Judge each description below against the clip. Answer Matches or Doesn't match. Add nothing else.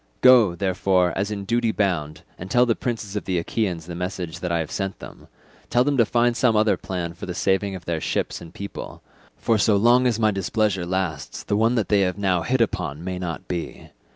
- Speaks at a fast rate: Matches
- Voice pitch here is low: Matches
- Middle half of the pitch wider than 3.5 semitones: Matches